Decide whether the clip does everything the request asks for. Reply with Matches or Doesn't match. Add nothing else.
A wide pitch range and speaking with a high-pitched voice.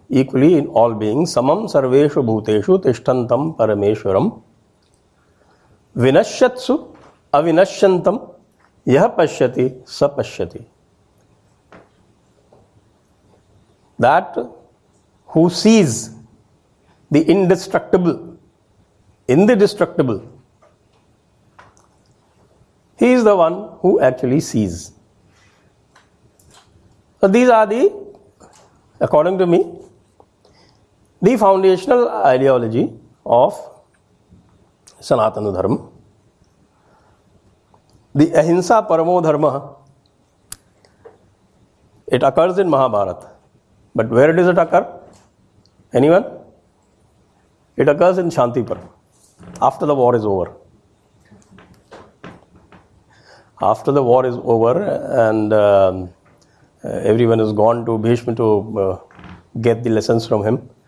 Doesn't match